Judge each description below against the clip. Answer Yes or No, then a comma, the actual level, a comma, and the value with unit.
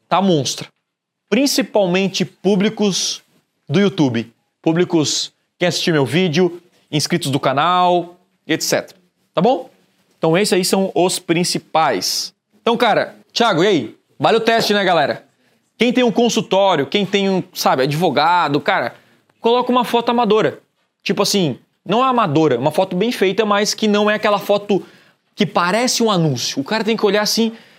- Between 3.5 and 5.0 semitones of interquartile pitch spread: Yes, average, 3.9 semitones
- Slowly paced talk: No, average, 155 wpm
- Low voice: No, high, 195 Hz